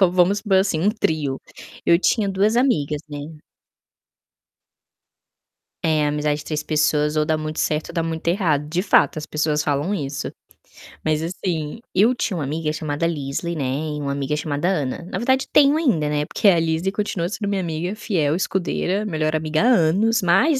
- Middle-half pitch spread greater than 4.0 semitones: Yes, average, 4.4 semitones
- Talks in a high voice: No, medium, 160 Hz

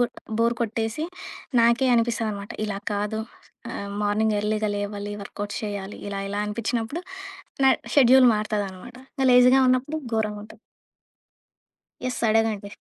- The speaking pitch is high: Yes, high, 220 Hz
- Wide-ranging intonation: No, average, 2.7 semitones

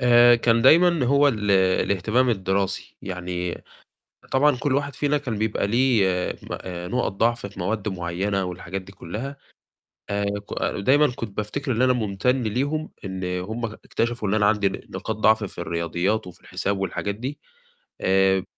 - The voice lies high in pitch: No, low, 105 Hz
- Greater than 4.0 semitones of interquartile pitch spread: Yes, average, 4.7 semitones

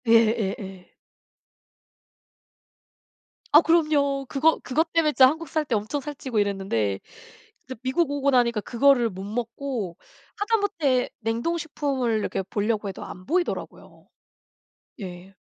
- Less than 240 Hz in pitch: No, very high, 255 Hz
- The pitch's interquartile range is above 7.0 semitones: No, wide, 6.0 semitones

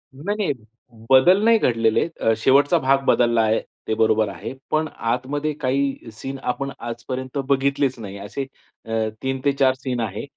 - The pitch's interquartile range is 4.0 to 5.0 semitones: No, average, 3.4 semitones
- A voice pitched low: Yes, low, 130 Hz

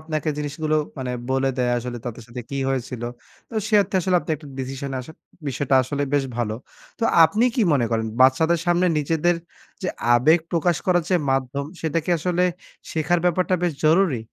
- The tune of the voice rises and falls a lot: No, average, 4.8 semitones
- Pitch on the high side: No, medium, 150 Hz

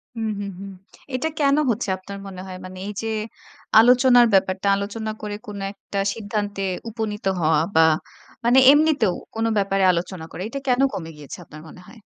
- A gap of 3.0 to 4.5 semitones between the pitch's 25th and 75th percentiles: Yes, average, 3.5 semitones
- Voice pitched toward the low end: No, high, 205 Hz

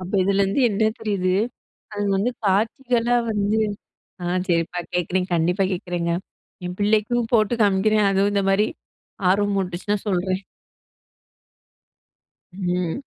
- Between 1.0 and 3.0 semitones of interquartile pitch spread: Yes, narrow, 2.6 semitones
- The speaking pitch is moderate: No, high, 195 Hz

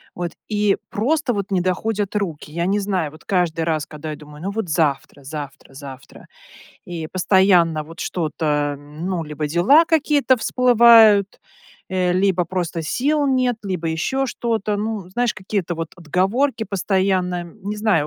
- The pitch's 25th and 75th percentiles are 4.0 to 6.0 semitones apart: Yes, average, 4.8 semitones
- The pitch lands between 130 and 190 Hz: Yes, medium, 185 Hz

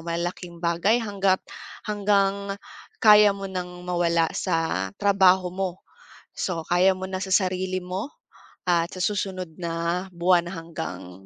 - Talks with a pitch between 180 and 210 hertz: Yes, medium, 185 Hz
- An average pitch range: No, narrow, 2.2 semitones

